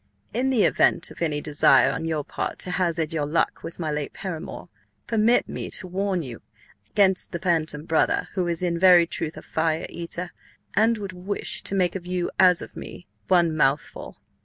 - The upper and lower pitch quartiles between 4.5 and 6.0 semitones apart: No, average, 2.8 semitones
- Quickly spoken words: No, average, 190 wpm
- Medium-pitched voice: Yes, medium, 175 Hz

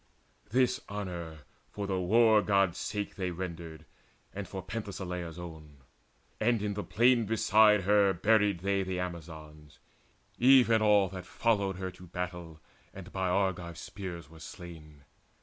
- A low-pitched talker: Yes, very low, 95 Hz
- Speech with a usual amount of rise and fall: Yes, average, 3.3 semitones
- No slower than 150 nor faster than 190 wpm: No, average, 140 wpm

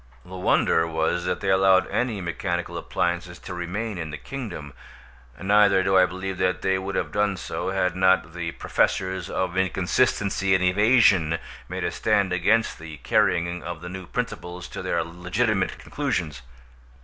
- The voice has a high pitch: No, very low, 95 Hz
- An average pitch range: No, narrow, 1.9 semitones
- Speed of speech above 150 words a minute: Yes, average, 160 wpm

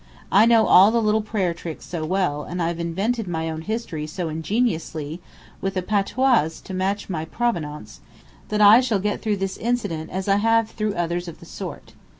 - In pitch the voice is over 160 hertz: Yes, high, 190 Hz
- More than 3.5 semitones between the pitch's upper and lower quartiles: Yes, average, 4.6 semitones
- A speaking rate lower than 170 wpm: No, average, 190 wpm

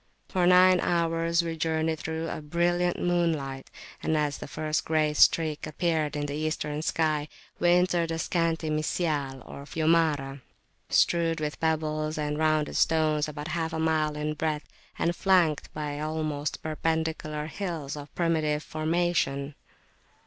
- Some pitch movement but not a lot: No, narrow, 1.7 semitones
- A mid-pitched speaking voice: Yes, medium, 155 Hz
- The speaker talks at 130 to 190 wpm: Yes, average, 140 wpm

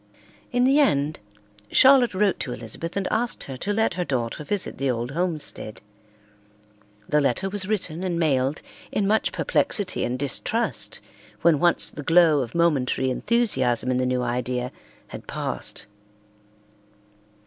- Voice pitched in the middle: Yes, medium, 155 Hz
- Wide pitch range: Yes, wide, 7.5 semitones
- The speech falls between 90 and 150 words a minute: Yes, average, 145 wpm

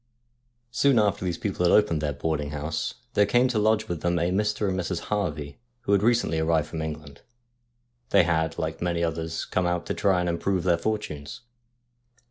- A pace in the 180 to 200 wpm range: Yes, average, 190 wpm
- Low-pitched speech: Yes, very low, 85 Hz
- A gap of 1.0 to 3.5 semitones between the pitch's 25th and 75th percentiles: No, average, 4.4 semitones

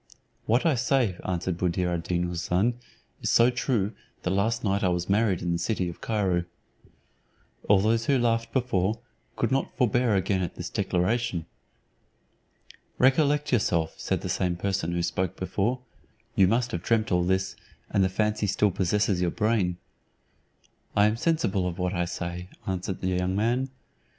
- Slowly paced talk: No, average, 165 wpm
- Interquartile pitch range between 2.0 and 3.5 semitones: No, average, 4.3 semitones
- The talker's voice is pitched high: No, low, 100 Hz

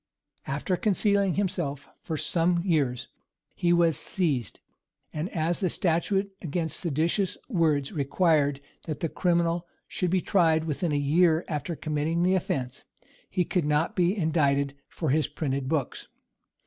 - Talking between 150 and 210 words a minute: No, average, 140 wpm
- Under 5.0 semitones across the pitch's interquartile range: Yes, average, 3.4 semitones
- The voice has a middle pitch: Yes, medium, 165 Hz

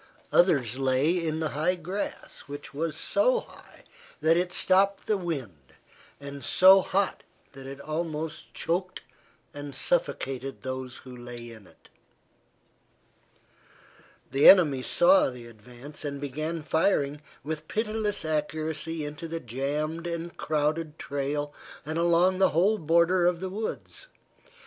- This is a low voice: No, medium, 155 Hz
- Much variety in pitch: No, average, 4.1 semitones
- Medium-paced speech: No, slow, 130 wpm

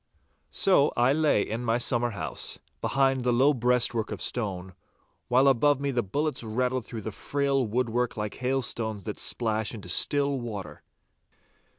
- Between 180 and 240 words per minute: No, average, 155 wpm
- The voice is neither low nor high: No, low, 120 Hz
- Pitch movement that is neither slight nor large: Yes, average, 3.4 semitones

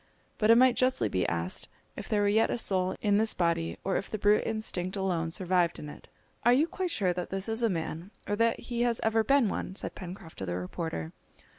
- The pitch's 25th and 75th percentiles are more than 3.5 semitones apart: Yes, average, 4.8 semitones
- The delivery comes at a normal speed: No, fast, 235 wpm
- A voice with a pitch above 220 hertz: No, high, 195 Hz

